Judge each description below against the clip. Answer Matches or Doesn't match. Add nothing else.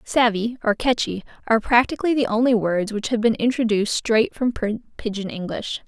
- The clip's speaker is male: Doesn't match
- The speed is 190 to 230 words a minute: Doesn't match